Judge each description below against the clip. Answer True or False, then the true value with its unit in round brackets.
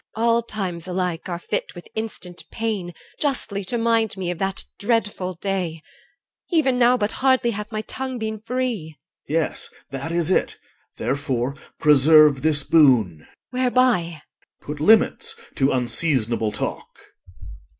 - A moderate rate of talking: True (150 wpm)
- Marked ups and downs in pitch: True (6.7 semitones)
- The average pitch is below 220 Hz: True (185 Hz)